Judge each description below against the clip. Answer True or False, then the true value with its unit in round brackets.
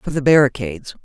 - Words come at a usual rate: True (175 wpm)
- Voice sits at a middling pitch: True (145 Hz)